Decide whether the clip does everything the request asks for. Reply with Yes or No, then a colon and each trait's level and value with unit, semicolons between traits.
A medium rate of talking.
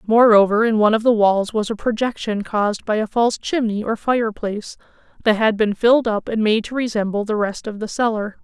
No: fast, 215 wpm